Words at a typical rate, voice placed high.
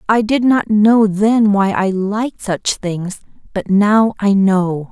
Yes: average, 170 wpm; high, 205 Hz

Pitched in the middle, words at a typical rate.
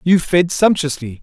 Yes: medium, 165 Hz; average, 145 wpm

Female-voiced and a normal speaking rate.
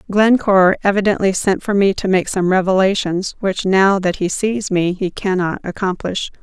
Yes: female; average, 170 wpm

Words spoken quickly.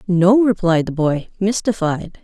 No: slow, 135 wpm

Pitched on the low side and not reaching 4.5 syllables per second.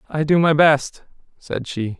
No: medium, 145 Hz; 4.0 syllables/s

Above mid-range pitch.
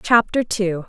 Yes: high, 205 Hz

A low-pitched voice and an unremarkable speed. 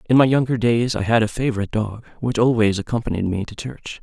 No: low, 115 Hz; fast, 225 wpm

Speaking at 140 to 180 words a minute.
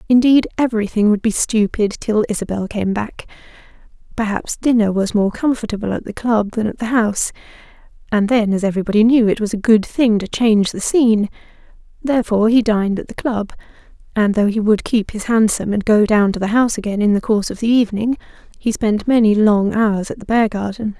No: average, 195 wpm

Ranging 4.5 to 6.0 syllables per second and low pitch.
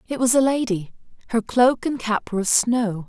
No: 5.1 syllables/s; high, 230 Hz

